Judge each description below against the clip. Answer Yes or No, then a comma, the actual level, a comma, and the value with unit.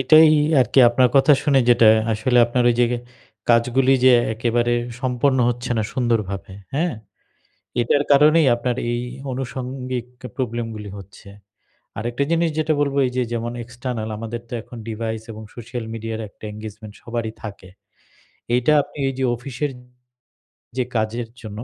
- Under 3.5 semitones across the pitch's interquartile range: Yes, average, 2.7 semitones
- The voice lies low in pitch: Yes, low, 120 Hz